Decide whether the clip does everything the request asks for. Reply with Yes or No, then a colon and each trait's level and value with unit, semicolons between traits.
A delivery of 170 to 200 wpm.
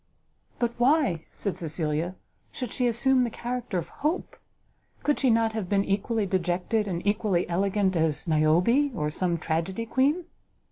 No: average, 150 wpm